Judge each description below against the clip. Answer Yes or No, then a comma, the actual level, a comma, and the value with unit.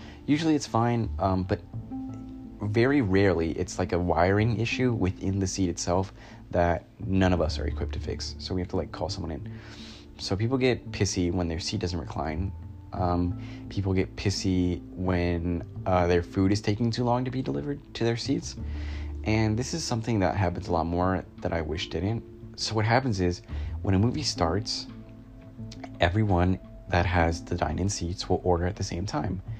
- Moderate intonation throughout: Yes, average, 4.4 semitones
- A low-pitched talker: Yes, very low, 95 Hz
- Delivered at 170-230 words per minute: Yes, average, 185 wpm